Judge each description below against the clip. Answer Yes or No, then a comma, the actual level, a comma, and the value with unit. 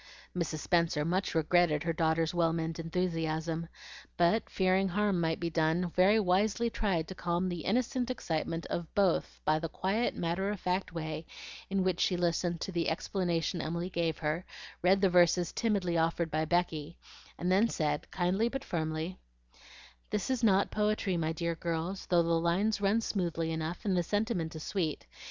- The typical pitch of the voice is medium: Yes, medium, 175 Hz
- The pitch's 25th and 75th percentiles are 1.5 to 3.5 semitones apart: Yes, average, 2.8 semitones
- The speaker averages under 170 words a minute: No, average, 175 wpm